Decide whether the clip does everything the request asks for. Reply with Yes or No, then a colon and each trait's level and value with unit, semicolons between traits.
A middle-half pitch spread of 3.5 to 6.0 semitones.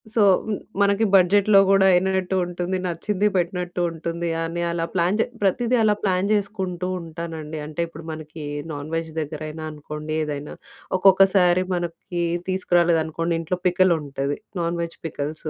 No: average, 2.9 semitones